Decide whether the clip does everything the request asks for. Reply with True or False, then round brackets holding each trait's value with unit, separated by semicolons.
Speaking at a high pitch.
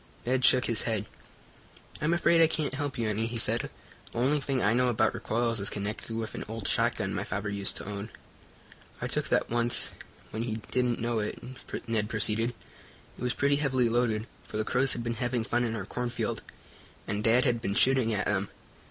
False (115 Hz)